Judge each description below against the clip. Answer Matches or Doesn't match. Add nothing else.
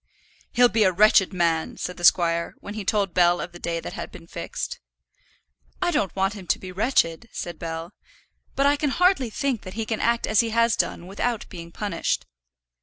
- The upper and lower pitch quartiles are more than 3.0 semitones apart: Matches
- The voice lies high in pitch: Matches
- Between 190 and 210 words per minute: Matches